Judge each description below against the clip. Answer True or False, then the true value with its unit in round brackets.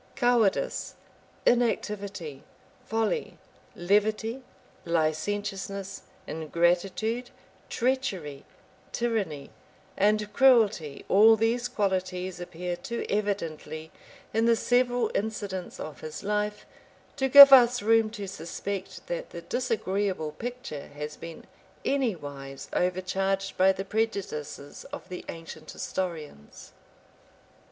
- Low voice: False (195 Hz)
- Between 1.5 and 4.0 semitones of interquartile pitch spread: False (5.0 semitones)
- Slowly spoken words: True (95 wpm)